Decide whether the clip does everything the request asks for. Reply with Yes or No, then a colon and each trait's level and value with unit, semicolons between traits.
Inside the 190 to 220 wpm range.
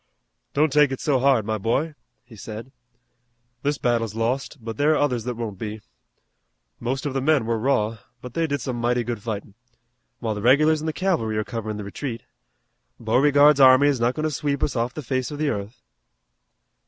Yes: average, 200 wpm